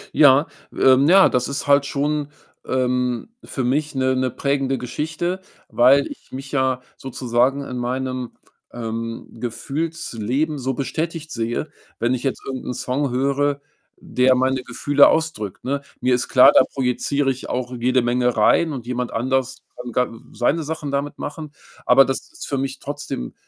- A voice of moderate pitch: No, low, 130 Hz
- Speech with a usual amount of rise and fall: No, narrow, 2.3 semitones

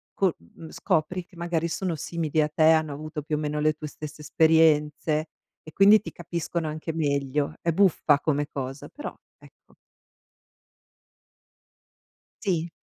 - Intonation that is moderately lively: No, narrow, 2.1 semitones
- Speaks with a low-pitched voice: No, medium, 155 Hz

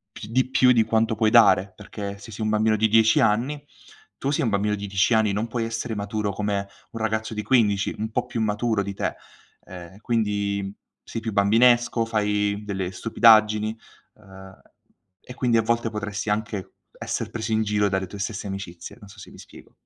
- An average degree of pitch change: No, narrow, 2.0 semitones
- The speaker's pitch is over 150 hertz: No, low, 105 Hz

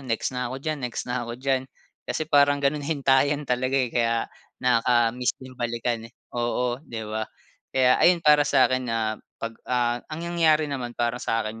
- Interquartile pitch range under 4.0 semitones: Yes, average, 3.0 semitones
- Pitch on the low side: Yes, low, 125 Hz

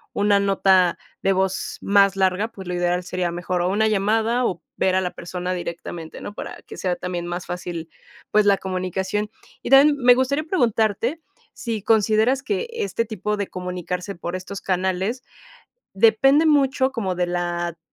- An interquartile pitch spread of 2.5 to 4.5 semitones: Yes, average, 3.8 semitones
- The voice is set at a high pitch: Yes, high, 195 Hz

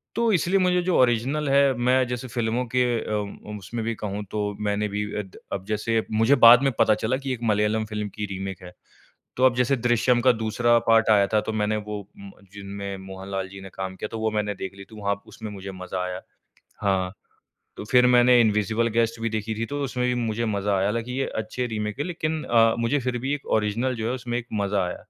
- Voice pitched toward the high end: No, low, 110 Hz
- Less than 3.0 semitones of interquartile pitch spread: No, average, 3.3 semitones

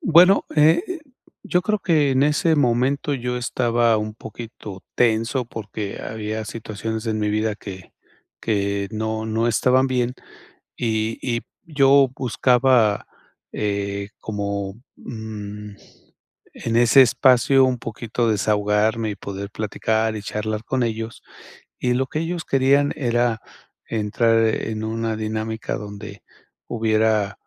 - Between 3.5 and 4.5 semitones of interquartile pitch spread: No, average, 3.0 semitones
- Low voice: Yes, low, 115 Hz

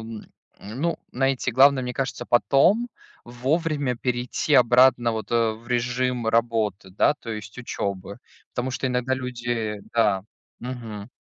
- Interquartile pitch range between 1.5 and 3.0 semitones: Yes, narrow, 2.5 semitones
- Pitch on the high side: No, low, 120 Hz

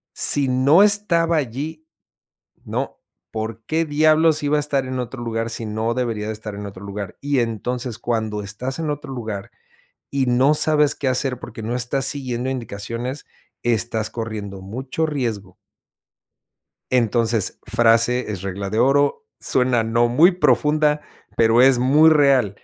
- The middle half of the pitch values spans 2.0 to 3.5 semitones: No, average, 4.3 semitones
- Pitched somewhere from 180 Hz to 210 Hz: No, low, 125 Hz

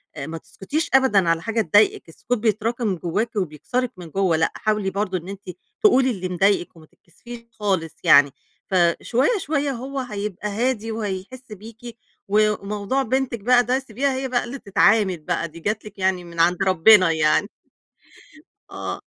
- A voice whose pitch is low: No, high, 210 Hz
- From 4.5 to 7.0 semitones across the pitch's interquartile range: Yes, average, 4.8 semitones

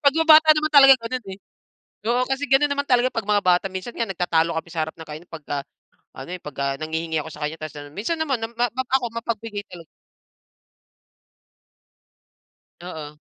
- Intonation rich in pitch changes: Yes, wide, 8.0 semitones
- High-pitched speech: Yes, high, 210 Hz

